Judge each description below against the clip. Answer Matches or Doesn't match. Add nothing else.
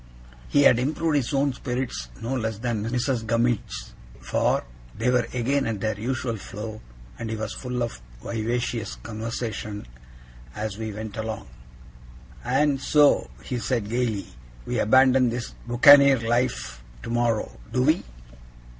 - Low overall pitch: Matches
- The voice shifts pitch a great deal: Doesn't match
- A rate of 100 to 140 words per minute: Matches